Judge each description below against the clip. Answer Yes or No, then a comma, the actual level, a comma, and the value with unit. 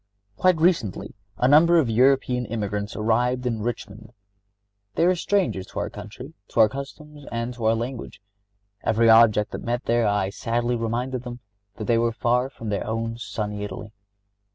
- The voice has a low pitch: Yes, low, 115 Hz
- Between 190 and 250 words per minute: No, average, 170 wpm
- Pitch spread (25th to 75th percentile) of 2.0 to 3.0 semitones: Yes, narrow, 2.6 semitones